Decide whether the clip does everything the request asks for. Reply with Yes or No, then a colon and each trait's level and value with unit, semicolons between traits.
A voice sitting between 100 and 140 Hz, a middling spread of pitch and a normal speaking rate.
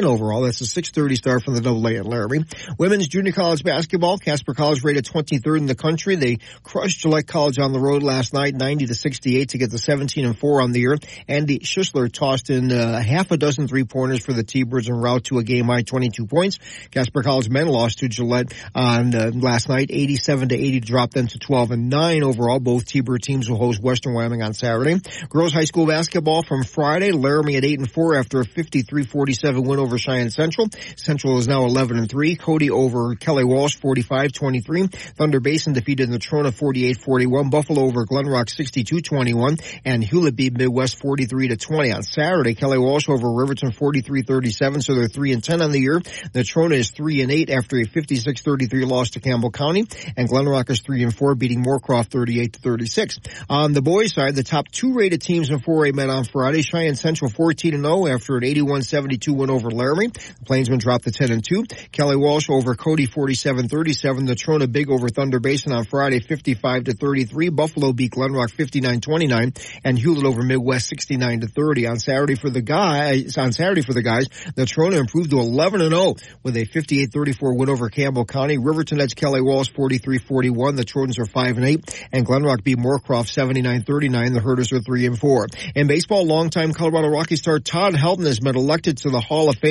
Yes: low, 135 Hz; average, 3.1 semitones; average, 195 wpm